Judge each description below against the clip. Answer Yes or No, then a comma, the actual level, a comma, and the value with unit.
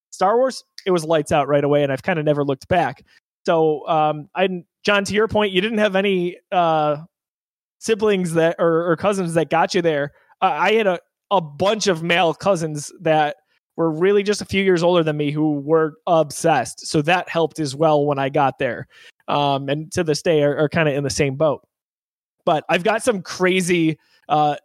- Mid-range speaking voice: Yes, medium, 165 Hz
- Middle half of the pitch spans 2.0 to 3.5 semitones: No, average, 3.9 semitones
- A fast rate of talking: Yes, fast, 210 wpm